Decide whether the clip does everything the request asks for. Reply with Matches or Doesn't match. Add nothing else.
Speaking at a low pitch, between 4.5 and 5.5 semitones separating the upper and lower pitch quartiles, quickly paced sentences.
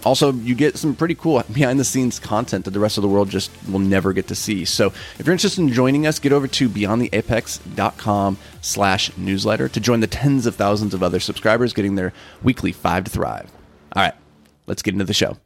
Matches